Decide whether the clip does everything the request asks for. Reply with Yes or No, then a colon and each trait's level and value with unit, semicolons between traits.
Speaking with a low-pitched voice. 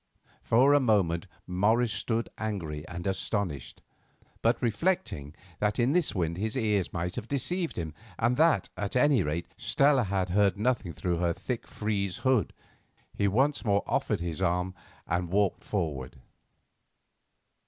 Yes: low, 100 Hz